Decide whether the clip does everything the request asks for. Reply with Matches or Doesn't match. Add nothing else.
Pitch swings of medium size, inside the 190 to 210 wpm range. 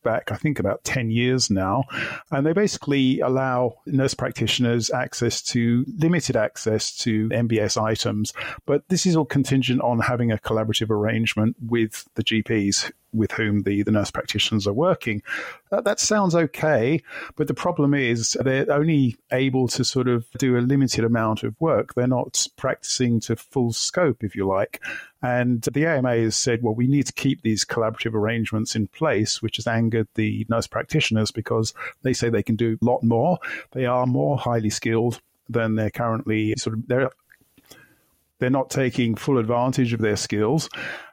Doesn't match